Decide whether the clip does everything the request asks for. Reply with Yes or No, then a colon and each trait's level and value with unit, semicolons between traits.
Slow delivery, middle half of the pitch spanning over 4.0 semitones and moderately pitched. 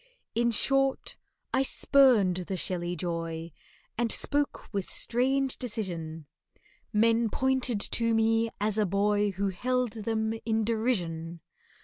No: slow, 120 wpm; average, 4.5 semitones; high, 220 Hz